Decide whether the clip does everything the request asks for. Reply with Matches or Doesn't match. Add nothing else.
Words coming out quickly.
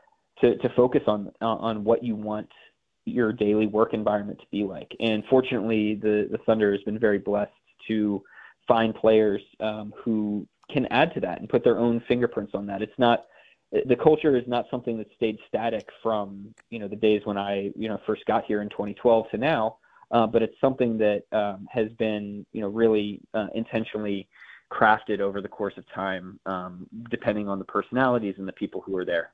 Doesn't match